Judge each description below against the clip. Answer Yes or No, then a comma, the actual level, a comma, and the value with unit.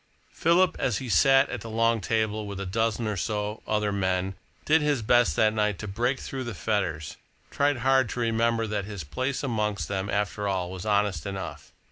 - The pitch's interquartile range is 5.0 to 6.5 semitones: No, average, 3.2 semitones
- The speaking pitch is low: Yes, low, 110 Hz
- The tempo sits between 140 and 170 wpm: No, average, 195 wpm